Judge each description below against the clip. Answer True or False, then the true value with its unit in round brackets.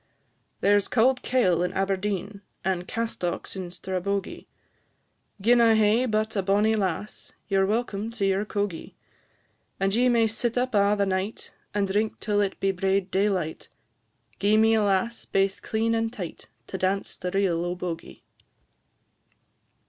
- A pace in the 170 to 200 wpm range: False (155 wpm)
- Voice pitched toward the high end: True (200 Hz)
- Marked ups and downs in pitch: False (2.5 semitones)